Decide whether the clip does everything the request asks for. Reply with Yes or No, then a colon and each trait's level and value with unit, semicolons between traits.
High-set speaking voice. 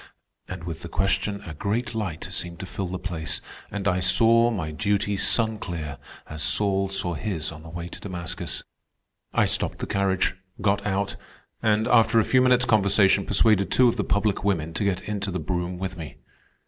No: very low, 95 Hz